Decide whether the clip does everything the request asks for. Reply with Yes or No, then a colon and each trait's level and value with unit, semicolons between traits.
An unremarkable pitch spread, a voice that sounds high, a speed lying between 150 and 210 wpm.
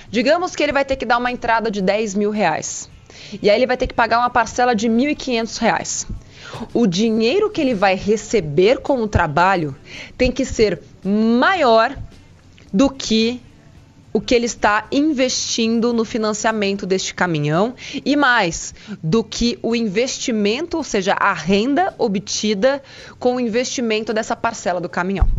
Yes: average, 3.8 semitones; high, 225 Hz; average, 160 wpm